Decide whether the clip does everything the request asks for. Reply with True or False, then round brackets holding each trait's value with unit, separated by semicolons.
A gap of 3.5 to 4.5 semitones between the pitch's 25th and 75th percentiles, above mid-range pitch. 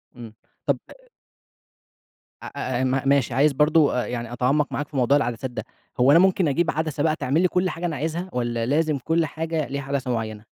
False (4.2 semitones; 140 Hz)